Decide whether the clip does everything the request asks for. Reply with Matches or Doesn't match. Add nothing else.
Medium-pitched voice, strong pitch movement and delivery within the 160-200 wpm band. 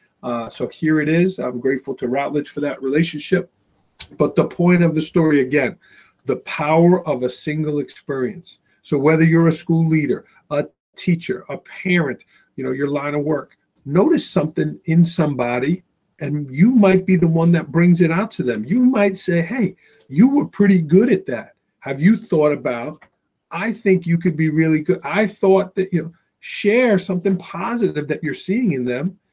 Doesn't match